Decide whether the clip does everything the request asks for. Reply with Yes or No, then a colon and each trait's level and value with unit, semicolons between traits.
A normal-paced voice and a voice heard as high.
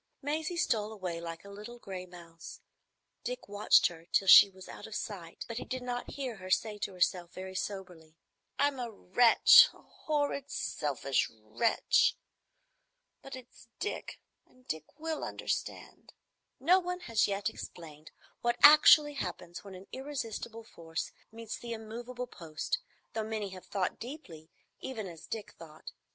Yes: average, 150 wpm; high, 215 Hz